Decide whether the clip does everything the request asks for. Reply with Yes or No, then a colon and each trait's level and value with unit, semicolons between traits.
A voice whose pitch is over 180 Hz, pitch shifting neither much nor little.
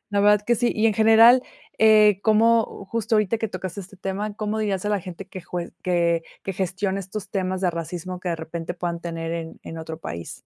Yes: high, 190 Hz; average, 3.8 semitones